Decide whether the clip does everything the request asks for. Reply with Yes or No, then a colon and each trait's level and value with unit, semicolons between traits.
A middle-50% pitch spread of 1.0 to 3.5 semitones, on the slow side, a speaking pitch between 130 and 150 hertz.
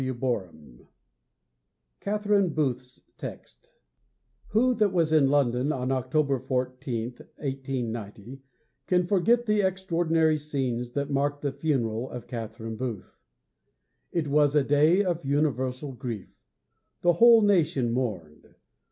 No: average, 5.0 semitones; slow, 115 wpm; medium, 140 Hz